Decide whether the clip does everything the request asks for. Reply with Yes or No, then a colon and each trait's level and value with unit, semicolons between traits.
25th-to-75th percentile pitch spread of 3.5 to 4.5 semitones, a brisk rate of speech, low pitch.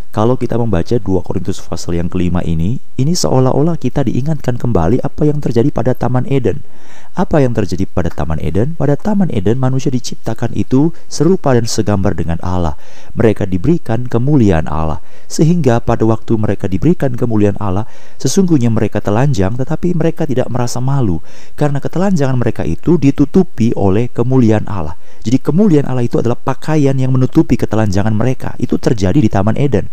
No: wide, 5.5 semitones; fast, 160 wpm; low, 120 Hz